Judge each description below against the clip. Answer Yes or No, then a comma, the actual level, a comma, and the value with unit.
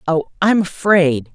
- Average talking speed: Yes, average, 180 wpm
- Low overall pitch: No, medium, 170 Hz